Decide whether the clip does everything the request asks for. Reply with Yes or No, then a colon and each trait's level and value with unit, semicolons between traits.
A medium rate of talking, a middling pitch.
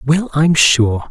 Yes: average, 165 wpm; medium, 145 Hz